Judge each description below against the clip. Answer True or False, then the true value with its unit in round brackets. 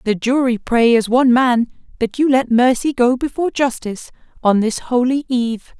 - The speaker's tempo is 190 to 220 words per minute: False (175 wpm)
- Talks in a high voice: True (245 Hz)